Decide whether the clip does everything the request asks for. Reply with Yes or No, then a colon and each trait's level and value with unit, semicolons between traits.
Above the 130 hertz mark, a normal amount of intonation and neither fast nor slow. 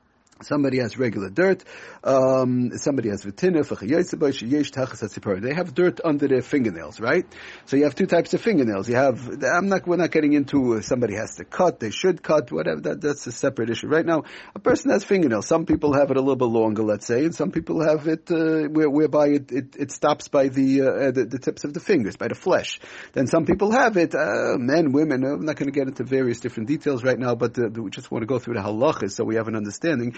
No: medium, 140 Hz; average, 4.5 semitones; fast, 230 wpm